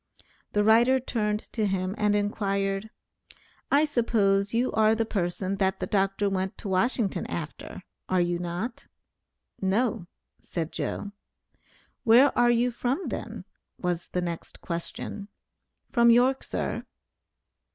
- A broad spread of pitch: No, average, 3.7 semitones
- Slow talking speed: Yes, slow, 130 wpm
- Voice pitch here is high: Yes, high, 205 Hz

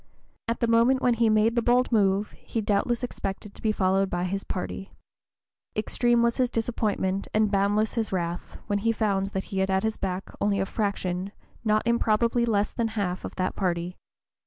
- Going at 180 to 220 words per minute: Yes, average, 190 wpm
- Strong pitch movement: No, average, 3.0 semitones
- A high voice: Yes, high, 210 Hz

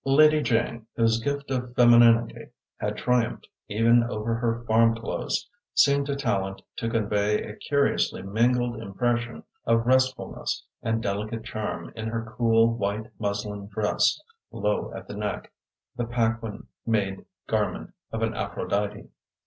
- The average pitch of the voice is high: No, low, 115 Hz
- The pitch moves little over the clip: Yes, narrow, 2.1 semitones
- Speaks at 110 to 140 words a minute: Yes, slow, 135 wpm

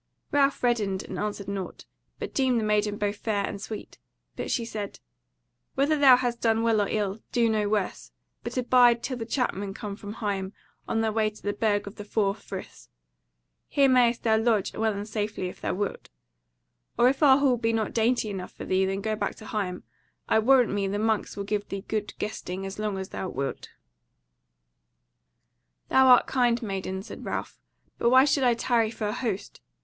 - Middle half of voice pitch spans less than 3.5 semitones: Yes, average, 2.9 semitones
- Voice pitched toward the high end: Yes, high, 215 Hz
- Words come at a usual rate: Yes, average, 195 wpm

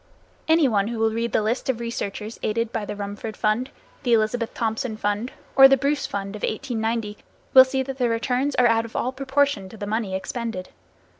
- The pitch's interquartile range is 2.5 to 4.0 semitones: Yes, average, 3.3 semitones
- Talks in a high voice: Yes, high, 230 Hz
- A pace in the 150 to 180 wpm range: No, fast, 205 wpm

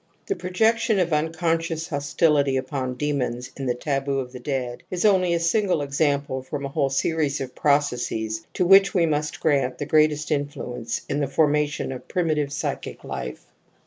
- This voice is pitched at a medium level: Yes, medium, 145 Hz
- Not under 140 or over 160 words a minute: No, average, 175 wpm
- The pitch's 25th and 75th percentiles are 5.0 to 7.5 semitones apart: No, average, 3.4 semitones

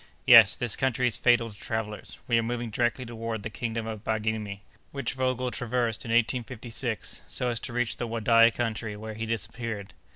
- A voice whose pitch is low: Yes, low, 115 Hz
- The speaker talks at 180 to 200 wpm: Yes, average, 185 wpm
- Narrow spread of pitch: Yes, narrow, 1.7 semitones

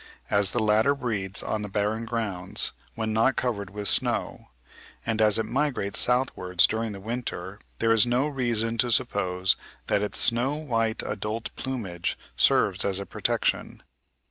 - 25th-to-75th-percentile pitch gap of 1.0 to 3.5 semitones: Yes, average, 3.0 semitones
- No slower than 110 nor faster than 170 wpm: Yes, average, 155 wpm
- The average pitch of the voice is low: Yes, low, 110 Hz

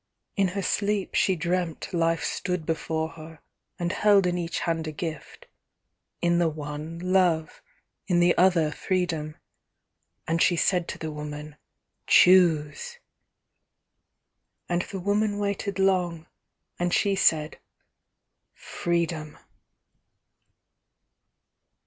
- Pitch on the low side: No, medium, 175 Hz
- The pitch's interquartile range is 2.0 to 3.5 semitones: Yes, average, 2.7 semitones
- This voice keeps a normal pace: No, slow, 110 wpm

